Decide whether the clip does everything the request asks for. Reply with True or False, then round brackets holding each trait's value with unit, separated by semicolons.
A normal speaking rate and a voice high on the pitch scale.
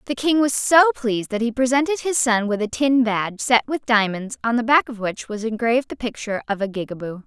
False (240 wpm; 240 Hz)